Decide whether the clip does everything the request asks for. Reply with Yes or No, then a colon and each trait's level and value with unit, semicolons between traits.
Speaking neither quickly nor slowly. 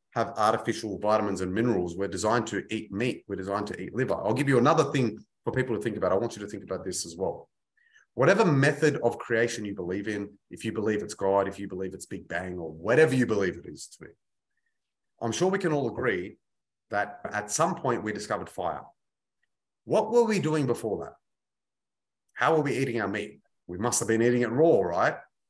No: fast, 220 wpm